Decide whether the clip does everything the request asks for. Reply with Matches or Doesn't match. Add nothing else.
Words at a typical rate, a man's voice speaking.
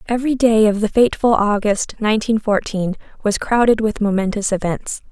Doesn't match